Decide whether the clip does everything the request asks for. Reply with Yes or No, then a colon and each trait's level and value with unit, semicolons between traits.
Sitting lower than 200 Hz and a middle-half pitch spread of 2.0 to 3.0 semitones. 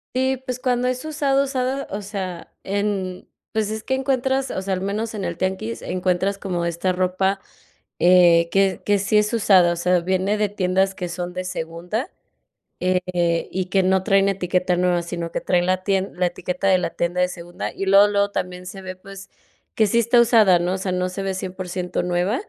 Yes: high, 190 Hz; narrow, 2.4 semitones